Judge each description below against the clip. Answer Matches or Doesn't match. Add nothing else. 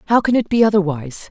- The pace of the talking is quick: Matches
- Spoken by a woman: Matches